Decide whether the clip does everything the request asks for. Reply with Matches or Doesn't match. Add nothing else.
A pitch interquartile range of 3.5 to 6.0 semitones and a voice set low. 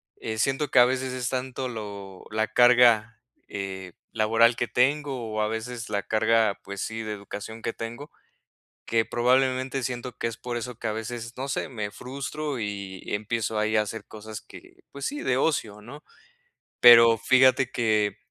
Doesn't match